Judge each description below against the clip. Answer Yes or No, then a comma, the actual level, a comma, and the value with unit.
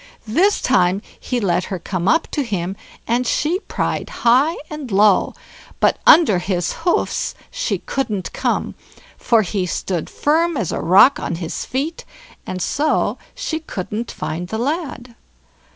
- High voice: Yes, high, 230 Hz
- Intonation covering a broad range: Yes, wide, 8.5 semitones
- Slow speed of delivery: No, average, 150 wpm